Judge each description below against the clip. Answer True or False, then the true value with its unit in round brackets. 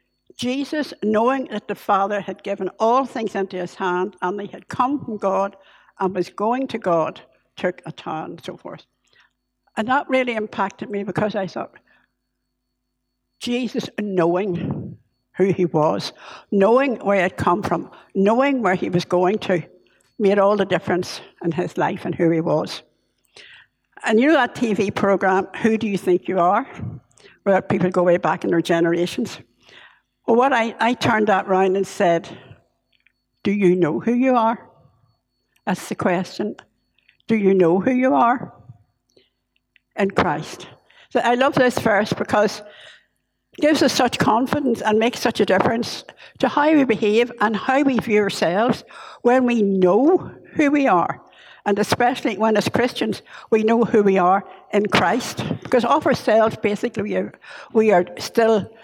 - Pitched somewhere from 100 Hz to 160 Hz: False (205 Hz)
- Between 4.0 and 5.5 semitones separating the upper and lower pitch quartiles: True (4.6 semitones)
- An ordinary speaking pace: True (165 wpm)